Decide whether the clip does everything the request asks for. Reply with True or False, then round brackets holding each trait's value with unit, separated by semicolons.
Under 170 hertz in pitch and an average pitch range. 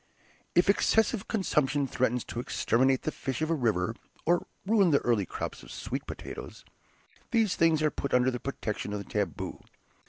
False (135 Hz; 6.0 semitones)